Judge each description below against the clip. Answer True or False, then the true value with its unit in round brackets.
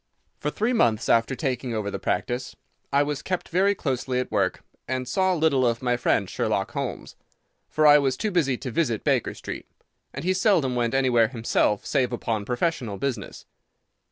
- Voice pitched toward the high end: False (130 Hz)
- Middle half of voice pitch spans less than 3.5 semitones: False (4.4 semitones)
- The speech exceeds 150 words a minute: True (180 wpm)